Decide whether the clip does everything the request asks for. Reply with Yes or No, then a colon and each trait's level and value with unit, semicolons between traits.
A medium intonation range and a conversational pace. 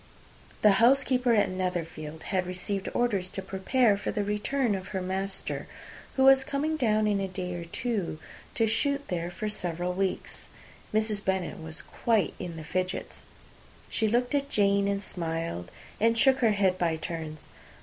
Yes: average, 4.0 semitones; average, 165 wpm